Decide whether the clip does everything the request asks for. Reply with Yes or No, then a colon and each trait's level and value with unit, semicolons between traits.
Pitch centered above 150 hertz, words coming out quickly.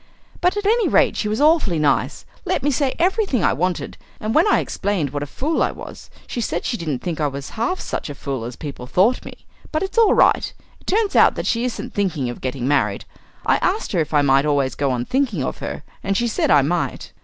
Yes: medium, 185 Hz; fast, 240 wpm